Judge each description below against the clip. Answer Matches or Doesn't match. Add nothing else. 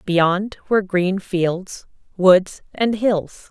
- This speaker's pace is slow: Matches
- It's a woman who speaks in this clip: Matches